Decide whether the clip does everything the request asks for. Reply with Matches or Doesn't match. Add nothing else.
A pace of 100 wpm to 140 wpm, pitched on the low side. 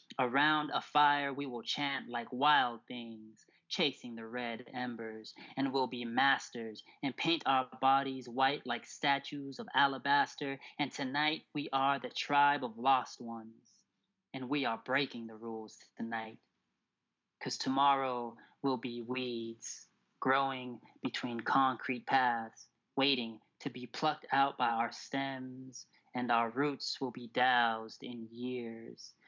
Matches